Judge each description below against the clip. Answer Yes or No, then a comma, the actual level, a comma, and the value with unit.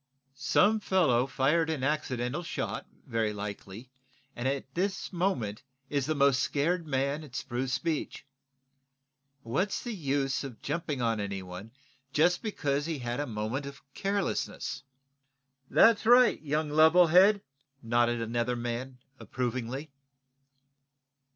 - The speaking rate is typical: No, slow, 125 wpm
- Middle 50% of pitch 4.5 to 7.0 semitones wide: Yes, average, 5.2 semitones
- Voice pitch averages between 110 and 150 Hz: Yes, medium, 140 Hz